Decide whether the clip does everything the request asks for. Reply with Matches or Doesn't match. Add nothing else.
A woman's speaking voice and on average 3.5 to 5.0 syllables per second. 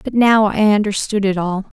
Matches